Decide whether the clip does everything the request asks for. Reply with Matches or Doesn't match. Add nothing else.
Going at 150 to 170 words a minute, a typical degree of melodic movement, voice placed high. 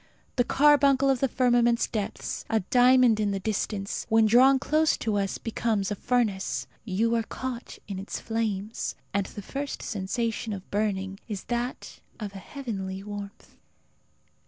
Matches